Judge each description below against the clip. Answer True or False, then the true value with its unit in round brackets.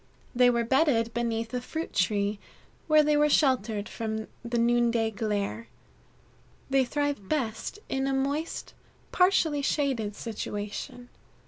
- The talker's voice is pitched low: False (240 Hz)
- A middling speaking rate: False (125 wpm)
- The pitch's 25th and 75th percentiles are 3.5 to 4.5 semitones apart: True (4.1 semitones)